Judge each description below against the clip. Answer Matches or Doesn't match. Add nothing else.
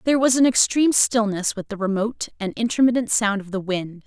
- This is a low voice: Doesn't match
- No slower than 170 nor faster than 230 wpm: Matches